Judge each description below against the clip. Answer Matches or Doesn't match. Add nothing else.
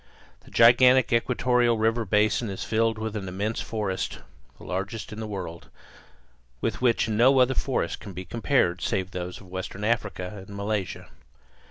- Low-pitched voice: Matches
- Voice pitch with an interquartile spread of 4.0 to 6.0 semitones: Doesn't match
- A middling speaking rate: Matches